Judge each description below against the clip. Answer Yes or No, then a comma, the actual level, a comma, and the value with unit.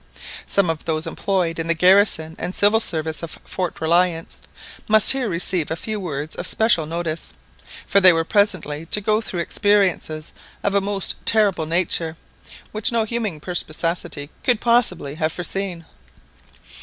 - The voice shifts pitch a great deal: No, average, 3.9 semitones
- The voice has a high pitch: No, medium, 180 Hz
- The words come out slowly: No, average, 155 wpm